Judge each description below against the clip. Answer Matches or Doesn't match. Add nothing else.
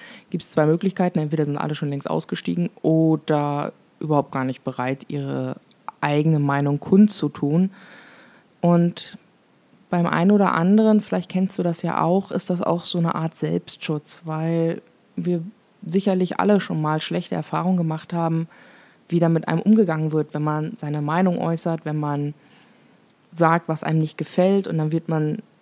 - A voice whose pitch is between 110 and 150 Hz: Doesn't match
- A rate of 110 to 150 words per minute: Doesn't match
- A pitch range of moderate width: Matches